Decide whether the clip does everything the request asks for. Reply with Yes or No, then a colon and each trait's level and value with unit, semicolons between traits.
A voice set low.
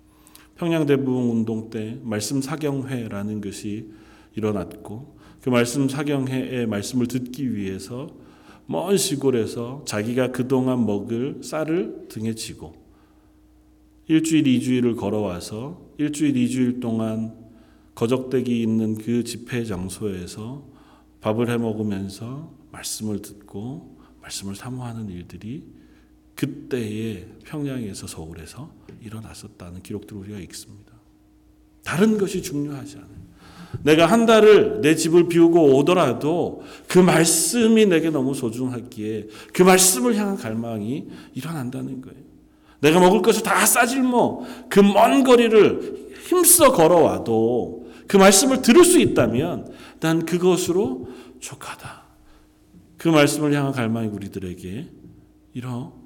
Yes: low, 120 Hz